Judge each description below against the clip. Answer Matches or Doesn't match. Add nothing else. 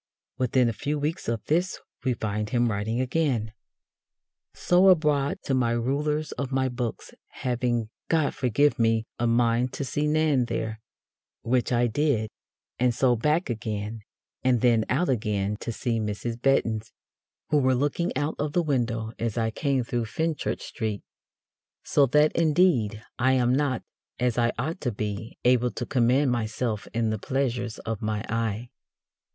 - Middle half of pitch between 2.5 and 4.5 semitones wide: Matches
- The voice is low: Matches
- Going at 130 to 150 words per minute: Doesn't match